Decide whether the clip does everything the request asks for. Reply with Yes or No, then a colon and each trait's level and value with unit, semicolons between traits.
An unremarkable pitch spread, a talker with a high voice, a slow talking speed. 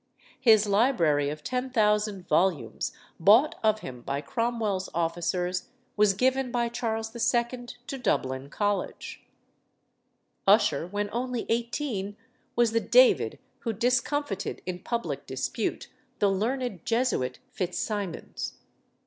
Yes: average, 4.5 semitones; high, 215 Hz; slow, 115 wpm